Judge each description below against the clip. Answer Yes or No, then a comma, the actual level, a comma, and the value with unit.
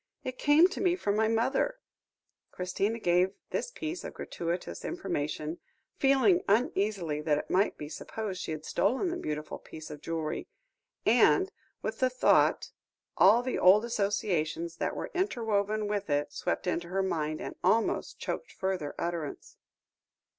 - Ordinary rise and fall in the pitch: No, wide, 6.4 semitones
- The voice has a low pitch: No, high, 195 Hz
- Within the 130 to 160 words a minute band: Yes, average, 150 wpm